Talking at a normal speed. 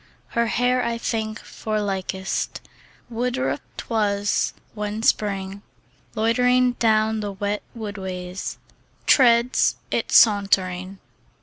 No: slow, 95 wpm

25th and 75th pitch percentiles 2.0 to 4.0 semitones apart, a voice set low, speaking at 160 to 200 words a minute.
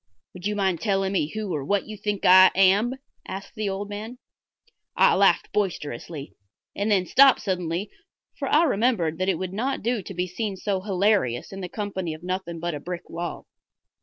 No: average, 2.8 semitones; high, 195 Hz; average, 195 wpm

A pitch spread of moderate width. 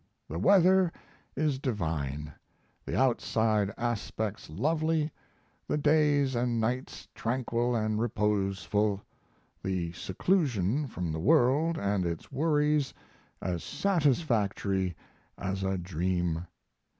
No: wide, 7.4 semitones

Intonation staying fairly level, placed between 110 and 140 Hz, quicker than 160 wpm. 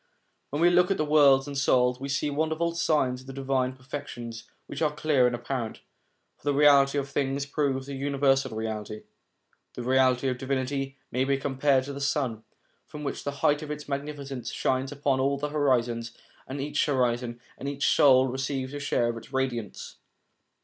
Yes: narrow, 2.0 semitones; low, 135 Hz; average, 190 wpm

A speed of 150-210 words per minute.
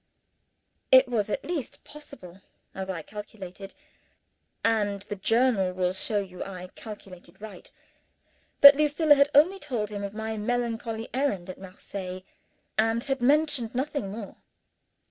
No: slow, 135 wpm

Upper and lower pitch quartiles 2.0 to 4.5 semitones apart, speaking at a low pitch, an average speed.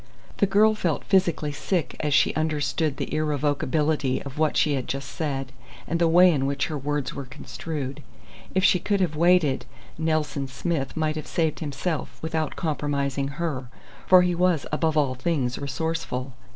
No: average, 3.0 semitones; medium, 150 Hz; average, 165 wpm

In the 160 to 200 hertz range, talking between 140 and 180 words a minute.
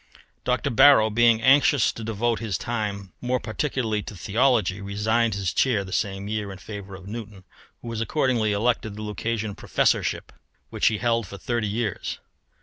No: low, 110 Hz; average, 170 wpm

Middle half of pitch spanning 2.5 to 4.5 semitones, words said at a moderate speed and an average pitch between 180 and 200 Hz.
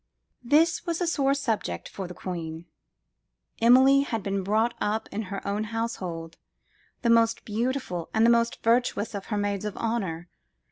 No: average, 3.4 semitones; average, 160 wpm; high, 220 Hz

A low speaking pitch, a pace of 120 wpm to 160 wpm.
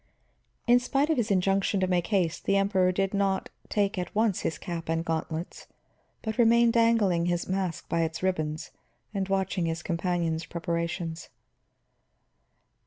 No: medium, 185 Hz; average, 150 wpm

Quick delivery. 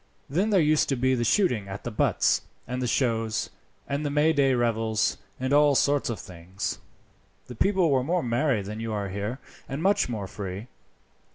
No: average, 185 wpm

